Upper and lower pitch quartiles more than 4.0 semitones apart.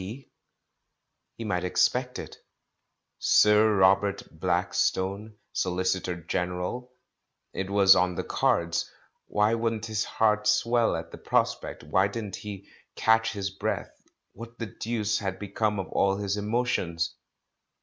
No: average, 3.0 semitones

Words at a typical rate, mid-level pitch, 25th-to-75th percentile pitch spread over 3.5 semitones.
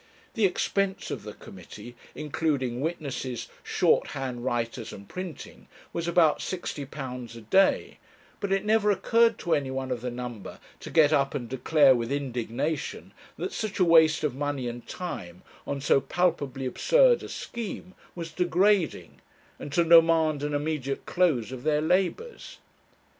Yes: average, 150 wpm; medium, 150 Hz; wide, 5.5 semitones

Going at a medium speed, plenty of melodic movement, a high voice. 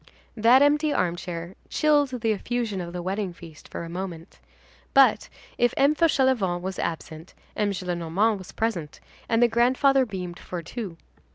Yes: average, 155 wpm; wide, 5.9 semitones; high, 200 Hz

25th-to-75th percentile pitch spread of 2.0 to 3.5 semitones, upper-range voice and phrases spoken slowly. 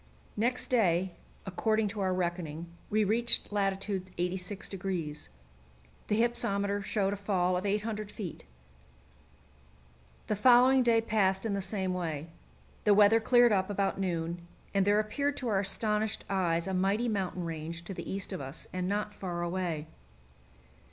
No: average, 2.9 semitones; high, 195 Hz; average, 150 wpm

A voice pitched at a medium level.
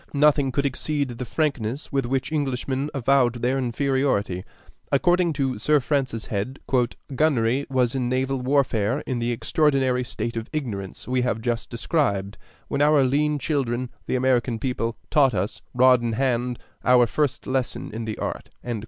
No: low, 130 Hz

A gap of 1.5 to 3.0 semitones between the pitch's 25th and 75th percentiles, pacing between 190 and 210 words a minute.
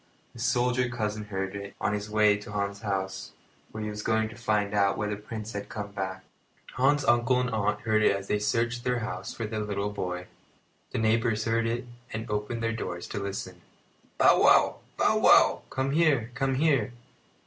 Yes: narrow, 2.6 semitones; average, 195 wpm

